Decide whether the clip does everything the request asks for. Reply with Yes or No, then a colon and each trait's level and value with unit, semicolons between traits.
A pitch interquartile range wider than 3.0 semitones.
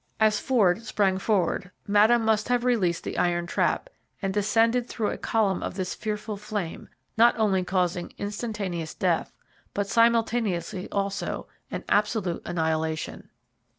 Yes: average, 3.6 semitones